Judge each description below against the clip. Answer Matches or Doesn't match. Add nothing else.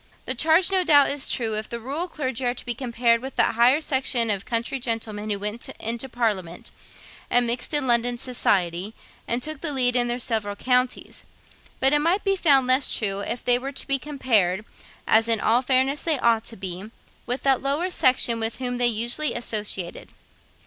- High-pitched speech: Matches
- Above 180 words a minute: Matches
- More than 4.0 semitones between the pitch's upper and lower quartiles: Doesn't match